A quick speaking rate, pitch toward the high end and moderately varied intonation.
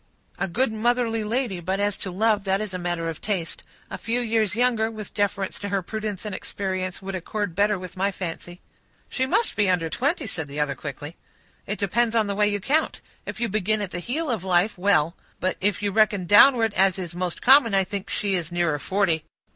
Yes: fast, 220 wpm; high, 200 Hz; average, 3.2 semitones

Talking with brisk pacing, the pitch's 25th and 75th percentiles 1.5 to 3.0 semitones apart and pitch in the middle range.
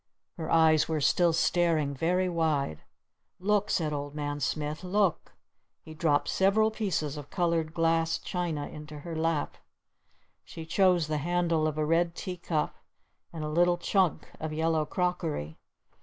No: average, 150 wpm; narrow, 2.5 semitones; medium, 165 Hz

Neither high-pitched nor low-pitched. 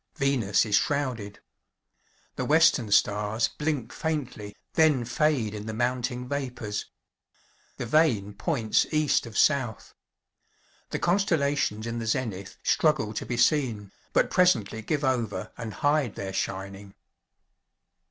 No: low, 120 Hz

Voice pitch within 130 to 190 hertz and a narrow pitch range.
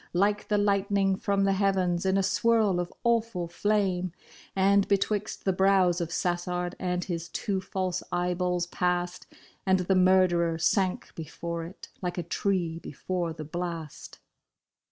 Yes: medium, 185 Hz; narrow, 2.0 semitones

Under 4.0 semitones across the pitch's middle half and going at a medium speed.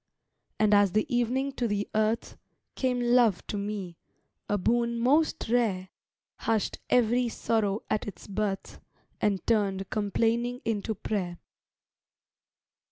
No: average, 2.9 semitones; slow, 120 wpm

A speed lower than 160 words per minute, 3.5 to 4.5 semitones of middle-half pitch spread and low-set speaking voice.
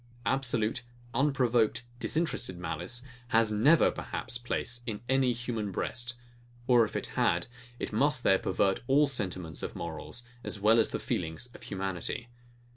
Yes: average, 145 wpm; average, 4.1 semitones; low, 115 Hz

